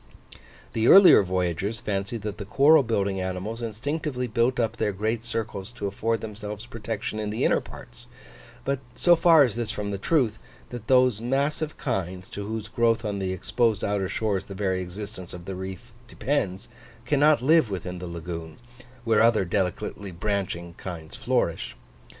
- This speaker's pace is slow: No, average, 165 wpm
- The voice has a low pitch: Yes, low, 105 Hz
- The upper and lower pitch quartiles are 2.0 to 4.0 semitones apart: Yes, average, 3.7 semitones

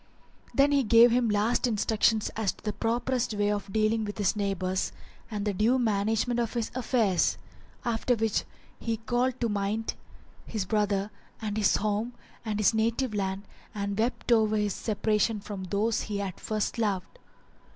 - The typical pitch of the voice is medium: No, high, 215 Hz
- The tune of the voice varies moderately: No, narrow, 2.2 semitones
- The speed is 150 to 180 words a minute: Yes, average, 170 wpm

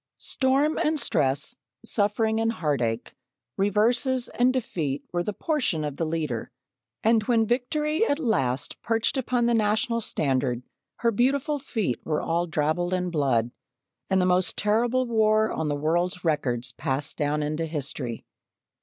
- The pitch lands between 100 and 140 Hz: No, medium, 185 Hz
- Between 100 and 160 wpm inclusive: Yes, average, 145 wpm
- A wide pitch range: Yes, wide, 7.9 semitones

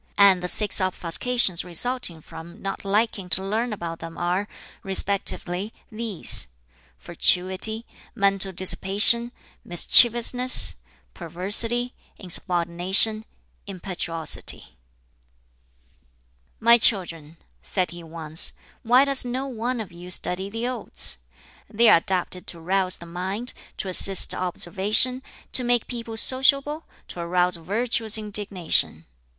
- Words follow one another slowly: Yes, slow, 110 wpm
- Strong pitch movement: No, average, 4.6 semitones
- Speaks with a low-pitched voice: No, high, 195 Hz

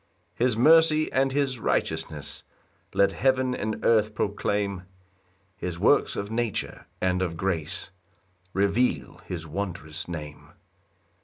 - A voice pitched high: No, low, 100 Hz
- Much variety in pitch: Yes, wide, 6.0 semitones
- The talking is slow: Yes, slow, 115 wpm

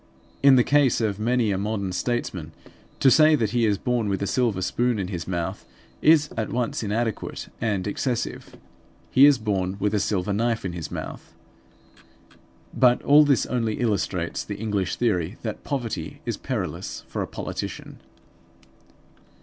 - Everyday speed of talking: Yes, average, 160 wpm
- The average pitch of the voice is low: Yes, low, 110 Hz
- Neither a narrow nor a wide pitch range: Yes, average, 3.8 semitones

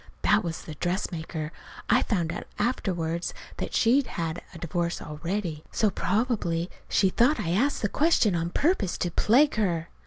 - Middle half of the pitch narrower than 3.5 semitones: No, average, 4.8 semitones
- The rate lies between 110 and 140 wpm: No, average, 160 wpm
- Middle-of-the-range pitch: Yes, medium, 180 Hz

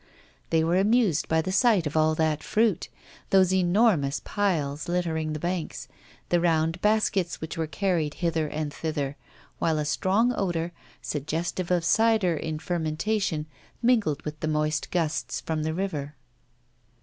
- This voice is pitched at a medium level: Yes, medium, 165 Hz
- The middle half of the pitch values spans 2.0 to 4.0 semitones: Yes, average, 3.4 semitones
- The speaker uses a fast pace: No, average, 150 wpm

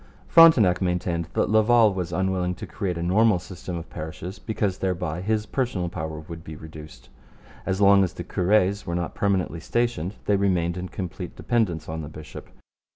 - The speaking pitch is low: Yes, very low, 90 Hz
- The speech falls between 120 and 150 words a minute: No, average, 175 wpm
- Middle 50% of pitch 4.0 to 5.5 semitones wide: No, average, 3.2 semitones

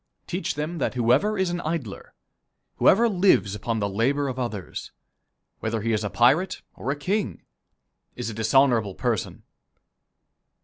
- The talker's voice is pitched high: No, low, 130 Hz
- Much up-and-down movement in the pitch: Yes, wide, 7.5 semitones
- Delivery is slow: No, average, 145 wpm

